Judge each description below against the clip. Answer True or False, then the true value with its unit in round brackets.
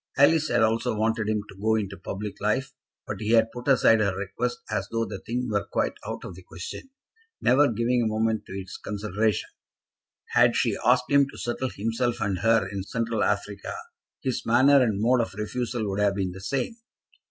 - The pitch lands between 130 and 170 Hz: False (110 Hz)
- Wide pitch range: False (3.2 semitones)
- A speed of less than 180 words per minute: False (200 wpm)